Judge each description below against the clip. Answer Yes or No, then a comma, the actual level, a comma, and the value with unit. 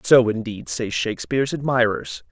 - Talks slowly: Yes, slow, 130 wpm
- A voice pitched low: Yes, low, 115 Hz